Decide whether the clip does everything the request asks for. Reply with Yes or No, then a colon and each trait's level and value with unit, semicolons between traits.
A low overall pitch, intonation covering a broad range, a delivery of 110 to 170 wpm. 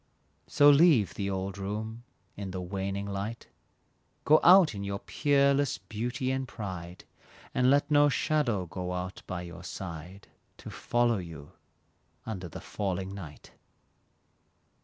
Yes: low, 100 Hz; wide, 6.0 semitones; slow, 135 wpm